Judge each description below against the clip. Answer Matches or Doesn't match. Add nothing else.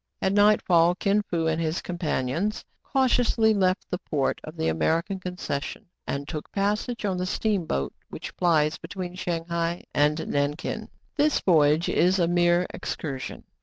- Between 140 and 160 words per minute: Matches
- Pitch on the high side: Doesn't match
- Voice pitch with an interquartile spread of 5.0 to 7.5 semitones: Doesn't match